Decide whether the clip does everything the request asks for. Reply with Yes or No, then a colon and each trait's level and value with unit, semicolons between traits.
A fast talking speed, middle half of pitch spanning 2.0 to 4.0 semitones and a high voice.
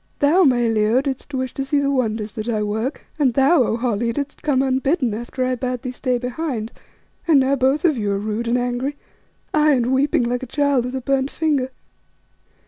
Yes: fast, 210 wpm; average, 2.9 semitones; very high, 255 Hz